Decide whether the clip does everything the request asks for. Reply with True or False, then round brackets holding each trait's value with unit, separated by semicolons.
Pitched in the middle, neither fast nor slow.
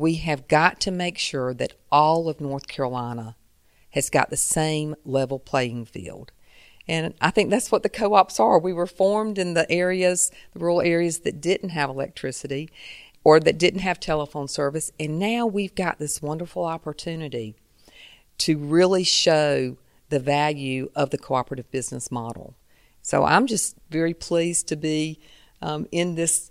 True (155 Hz; 165 wpm)